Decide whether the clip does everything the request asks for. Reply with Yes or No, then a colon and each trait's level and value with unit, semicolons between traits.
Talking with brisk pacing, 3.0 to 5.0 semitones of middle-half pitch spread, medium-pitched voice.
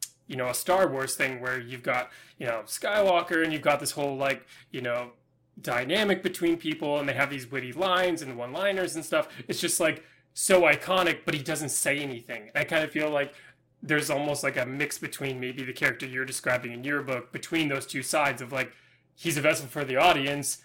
Yes: fast, 220 wpm; average, 3.5 semitones; medium, 145 Hz